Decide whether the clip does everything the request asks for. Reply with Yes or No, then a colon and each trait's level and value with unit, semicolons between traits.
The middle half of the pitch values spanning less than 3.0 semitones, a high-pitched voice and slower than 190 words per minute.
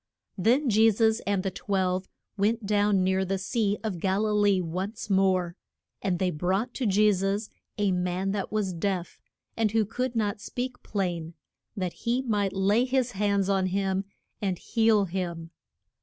Yes: narrow, 2.5 semitones; high, 200 Hz; average, 170 wpm